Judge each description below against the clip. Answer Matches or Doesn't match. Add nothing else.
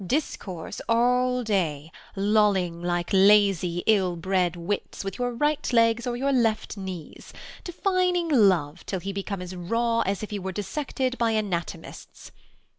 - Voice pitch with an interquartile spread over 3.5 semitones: Matches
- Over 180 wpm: Doesn't match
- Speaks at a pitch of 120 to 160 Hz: Doesn't match